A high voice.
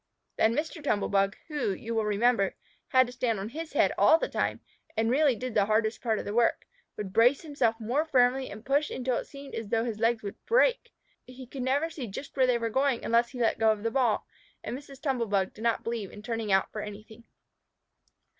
Yes: high, 235 Hz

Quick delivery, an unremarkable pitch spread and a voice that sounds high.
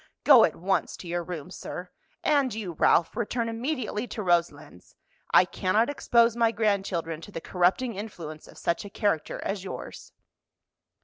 No: average, 160 wpm; average, 4.9 semitones; high, 195 Hz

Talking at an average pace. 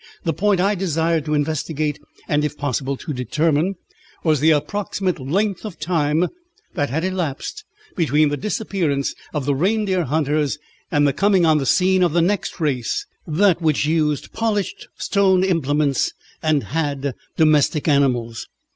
Yes: average, 150 wpm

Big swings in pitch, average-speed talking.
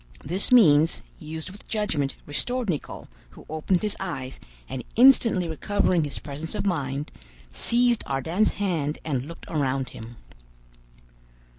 No: wide, 6.4 semitones; slow, 130 wpm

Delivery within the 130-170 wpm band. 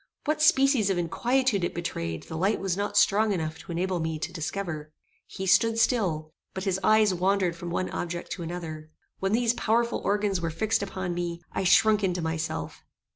No: average, 185 wpm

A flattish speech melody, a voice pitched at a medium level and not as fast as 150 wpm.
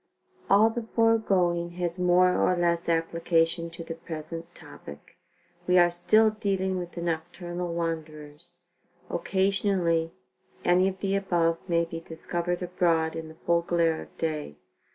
Yes: narrow, 1.7 semitones; medium, 175 Hz; average, 140 wpm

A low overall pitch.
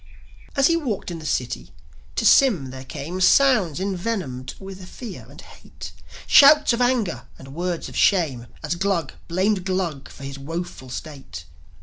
No: medium, 175 Hz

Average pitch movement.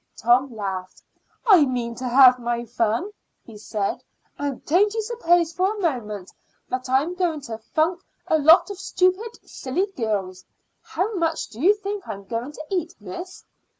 No: wide, 7.8 semitones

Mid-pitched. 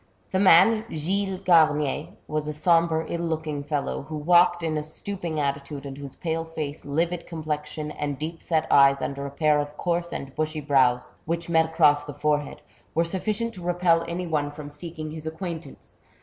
Yes: medium, 155 Hz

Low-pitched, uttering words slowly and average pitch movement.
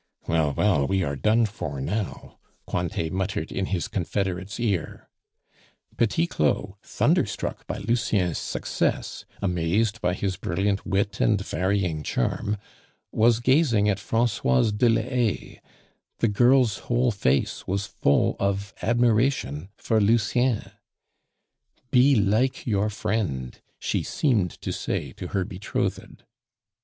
Yes: low, 100 Hz; slow, 125 wpm; average, 4.0 semitones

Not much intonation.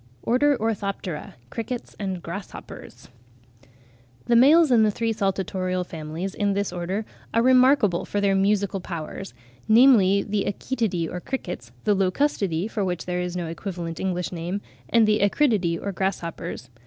No: average, 3.8 semitones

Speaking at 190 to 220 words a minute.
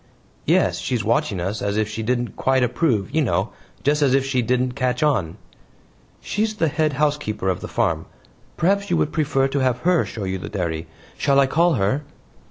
Yes: average, 195 wpm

